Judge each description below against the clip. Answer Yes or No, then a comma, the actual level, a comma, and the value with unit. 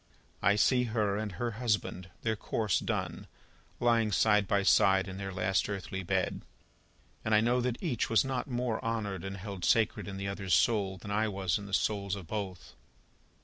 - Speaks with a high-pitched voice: No, low, 105 Hz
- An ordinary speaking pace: Yes, average, 190 wpm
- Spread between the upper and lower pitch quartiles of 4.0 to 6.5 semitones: No, narrow, 2.6 semitones